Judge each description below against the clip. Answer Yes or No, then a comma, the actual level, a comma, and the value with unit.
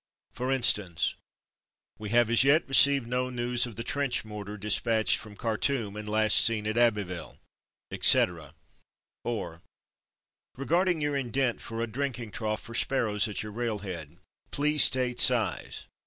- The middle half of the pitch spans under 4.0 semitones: Yes, average, 3.3 semitones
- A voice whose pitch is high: No, low, 115 Hz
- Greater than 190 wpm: No, average, 140 wpm